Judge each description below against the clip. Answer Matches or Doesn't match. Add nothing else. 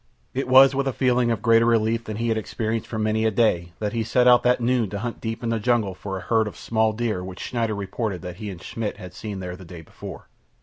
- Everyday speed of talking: Doesn't match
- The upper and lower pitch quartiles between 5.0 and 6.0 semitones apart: Doesn't match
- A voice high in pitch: Doesn't match